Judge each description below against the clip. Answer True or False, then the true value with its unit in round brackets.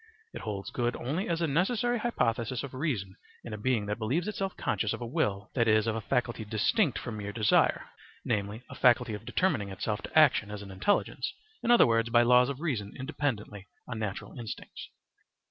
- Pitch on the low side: True (120 Hz)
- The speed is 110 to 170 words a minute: False (195 wpm)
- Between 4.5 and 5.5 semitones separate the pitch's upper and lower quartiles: True (5.1 semitones)